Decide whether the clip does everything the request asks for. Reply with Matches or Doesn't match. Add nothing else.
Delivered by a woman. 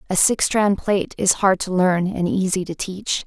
Matches